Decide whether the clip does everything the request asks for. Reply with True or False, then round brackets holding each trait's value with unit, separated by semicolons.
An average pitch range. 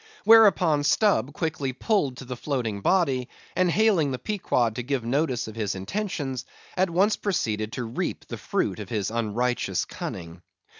False (7.4 semitones)